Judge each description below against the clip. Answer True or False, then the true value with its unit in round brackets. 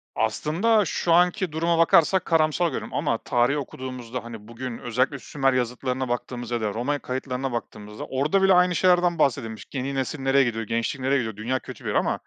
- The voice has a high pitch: False (130 Hz)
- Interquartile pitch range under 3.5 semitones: False (5.0 semitones)